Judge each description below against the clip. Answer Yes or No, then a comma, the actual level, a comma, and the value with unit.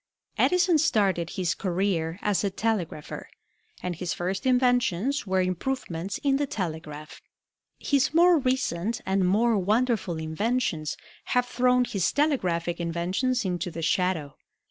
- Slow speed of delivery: Yes, slow, 125 wpm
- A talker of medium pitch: No, high, 195 Hz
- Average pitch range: No, wide, 6.5 semitones